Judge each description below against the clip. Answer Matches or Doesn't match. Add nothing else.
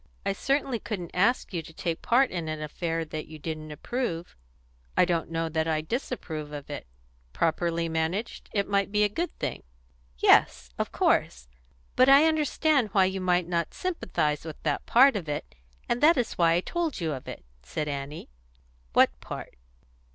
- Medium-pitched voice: Matches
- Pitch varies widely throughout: Matches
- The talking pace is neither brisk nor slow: Matches